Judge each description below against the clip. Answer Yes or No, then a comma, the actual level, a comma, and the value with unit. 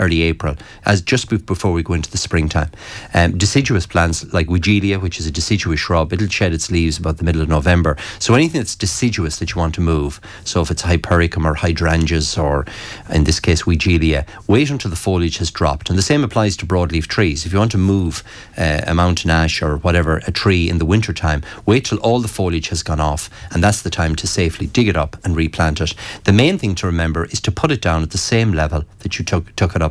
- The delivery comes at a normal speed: No, fast, 235 wpm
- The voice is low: Yes, very low, 90 Hz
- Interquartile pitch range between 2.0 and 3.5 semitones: No, average, 3.9 semitones